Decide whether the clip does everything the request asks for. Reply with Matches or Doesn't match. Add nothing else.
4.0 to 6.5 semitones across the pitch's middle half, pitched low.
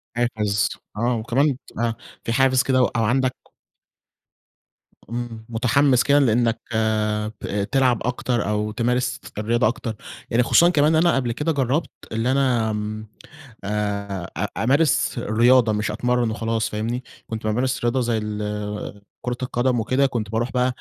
Doesn't match